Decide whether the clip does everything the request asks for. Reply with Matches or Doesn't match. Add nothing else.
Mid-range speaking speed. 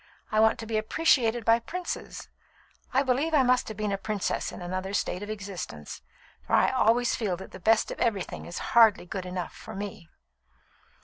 Matches